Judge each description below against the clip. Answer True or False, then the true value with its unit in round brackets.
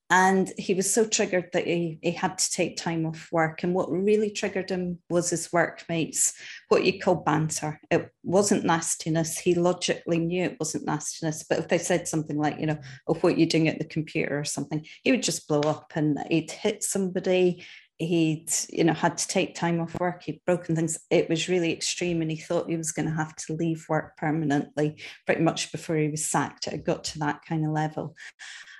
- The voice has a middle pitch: True (165 Hz)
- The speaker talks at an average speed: False (215 wpm)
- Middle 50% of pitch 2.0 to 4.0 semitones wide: True (2.4 semitones)